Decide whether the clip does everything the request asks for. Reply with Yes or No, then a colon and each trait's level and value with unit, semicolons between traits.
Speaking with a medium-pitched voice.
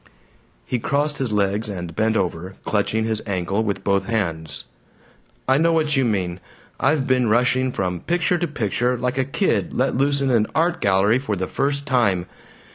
No: low, 115 Hz